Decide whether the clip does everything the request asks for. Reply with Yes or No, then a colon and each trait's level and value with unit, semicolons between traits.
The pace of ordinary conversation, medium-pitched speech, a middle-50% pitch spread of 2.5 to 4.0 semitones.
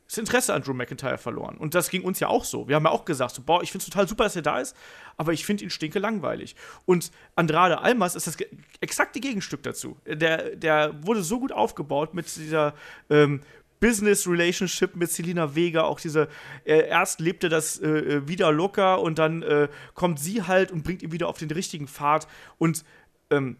No: fast, 205 wpm; medium, 165 Hz; average, 3.4 semitones